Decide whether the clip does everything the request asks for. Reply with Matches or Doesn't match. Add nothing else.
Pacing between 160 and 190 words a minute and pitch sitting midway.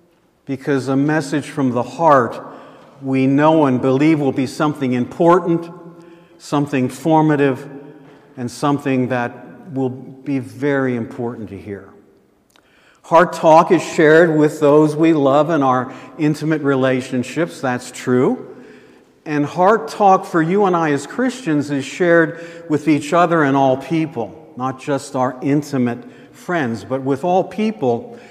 Doesn't match